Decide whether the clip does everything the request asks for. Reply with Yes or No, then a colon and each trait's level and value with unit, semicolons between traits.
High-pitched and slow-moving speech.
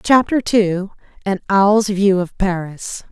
Yes: high, 195 Hz; slow, 115 wpm